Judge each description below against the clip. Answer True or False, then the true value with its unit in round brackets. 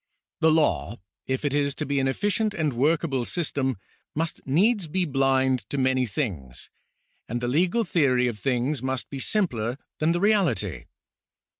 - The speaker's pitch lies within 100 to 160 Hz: True (140 Hz)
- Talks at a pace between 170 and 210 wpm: False (160 wpm)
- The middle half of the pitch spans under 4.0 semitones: False (4.5 semitones)